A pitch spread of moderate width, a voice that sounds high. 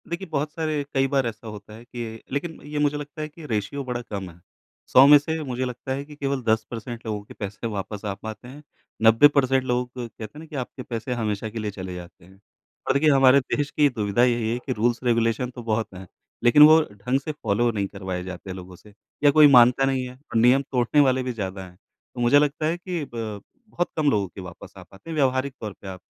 No: average, 4.8 semitones; low, 120 Hz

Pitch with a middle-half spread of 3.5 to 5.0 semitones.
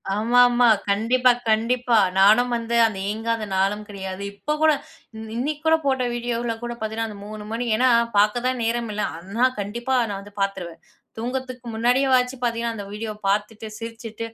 No: average, 2.7 semitones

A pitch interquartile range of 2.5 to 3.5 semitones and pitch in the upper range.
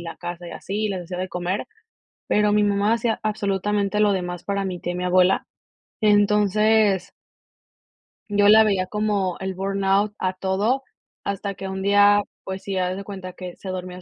No: narrow, 2.0 semitones; high, 195 Hz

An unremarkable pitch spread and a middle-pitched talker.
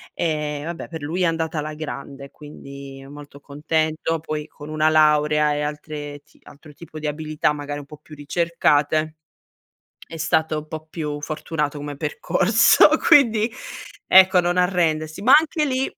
No: narrow, 1.9 semitones; medium, 155 Hz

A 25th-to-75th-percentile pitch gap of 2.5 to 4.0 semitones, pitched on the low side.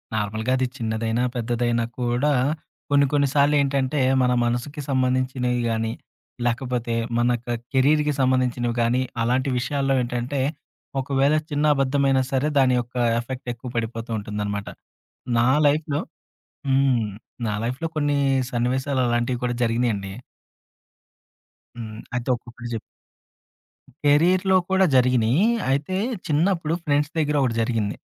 Yes: average, 3.1 semitones; low, 125 Hz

